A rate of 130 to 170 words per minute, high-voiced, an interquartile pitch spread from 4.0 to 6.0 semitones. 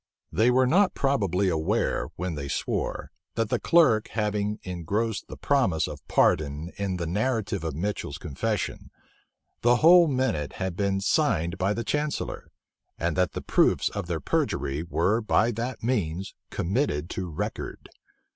No: average, 150 wpm; low, 100 Hz; wide, 5.6 semitones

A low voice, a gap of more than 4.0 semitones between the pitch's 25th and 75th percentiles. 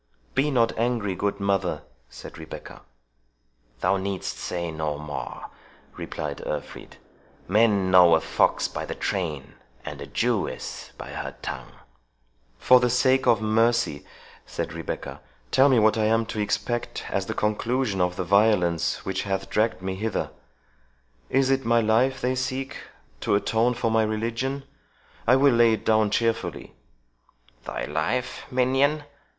Yes: low, 110 Hz; average, 4.6 semitones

